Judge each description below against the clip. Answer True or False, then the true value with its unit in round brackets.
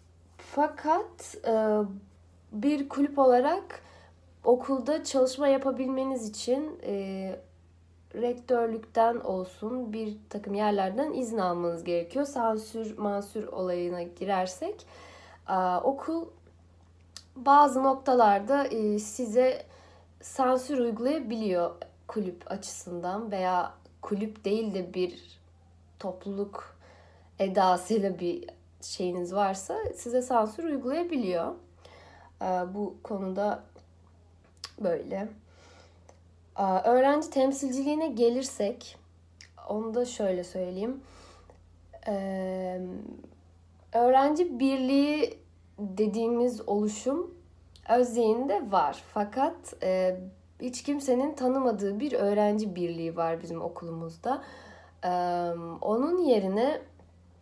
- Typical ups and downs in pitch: False (6.9 semitones)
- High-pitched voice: True (205 Hz)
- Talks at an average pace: False (70 wpm)